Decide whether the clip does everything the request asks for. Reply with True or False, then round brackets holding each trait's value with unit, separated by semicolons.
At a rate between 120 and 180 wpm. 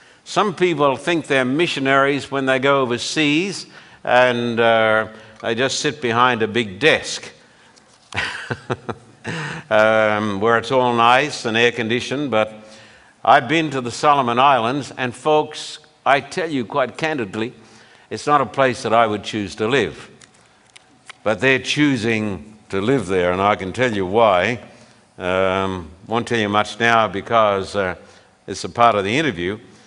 True (155 wpm)